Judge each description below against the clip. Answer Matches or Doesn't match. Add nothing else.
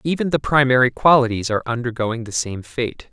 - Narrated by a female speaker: Doesn't match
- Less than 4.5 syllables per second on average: Doesn't match